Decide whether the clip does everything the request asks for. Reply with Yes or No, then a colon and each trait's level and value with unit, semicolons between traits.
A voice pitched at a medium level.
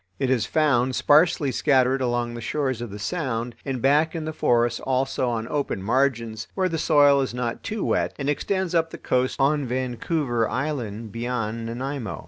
No: low, 130 Hz